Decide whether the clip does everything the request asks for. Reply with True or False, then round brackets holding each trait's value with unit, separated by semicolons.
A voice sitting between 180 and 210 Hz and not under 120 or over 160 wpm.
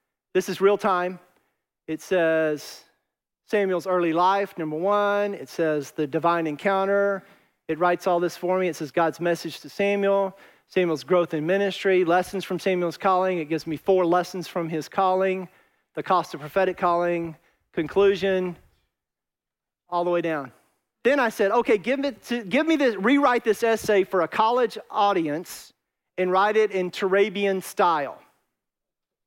True (185 Hz; 155 wpm)